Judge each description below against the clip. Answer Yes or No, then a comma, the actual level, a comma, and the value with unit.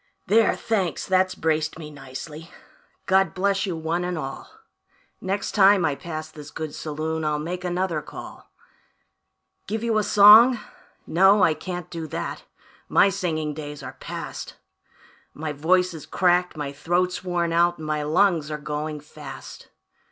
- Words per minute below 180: Yes, average, 150 wpm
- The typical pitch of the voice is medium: Yes, medium, 165 Hz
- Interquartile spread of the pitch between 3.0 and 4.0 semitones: Yes, average, 3.3 semitones